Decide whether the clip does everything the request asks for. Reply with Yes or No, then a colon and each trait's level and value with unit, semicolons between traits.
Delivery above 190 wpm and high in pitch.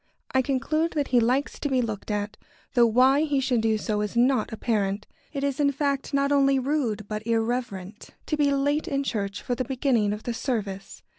Yes: fast, 205 wpm; very high, 250 Hz